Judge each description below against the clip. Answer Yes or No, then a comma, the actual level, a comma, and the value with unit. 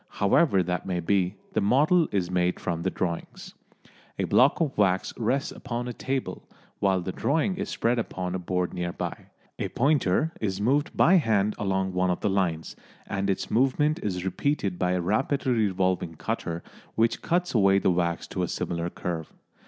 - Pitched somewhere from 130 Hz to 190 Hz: No, very low, 95 Hz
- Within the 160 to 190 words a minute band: Yes, average, 180 wpm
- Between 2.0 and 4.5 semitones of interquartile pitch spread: No, wide, 5.6 semitones